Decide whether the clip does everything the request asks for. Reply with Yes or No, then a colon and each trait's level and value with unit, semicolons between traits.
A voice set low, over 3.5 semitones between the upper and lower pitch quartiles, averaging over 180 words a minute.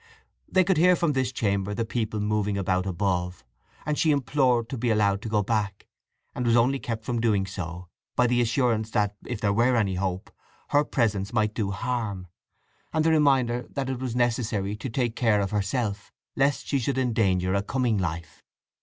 Yes: low, 110 Hz; average, 4.0 semitones; average, 190 wpm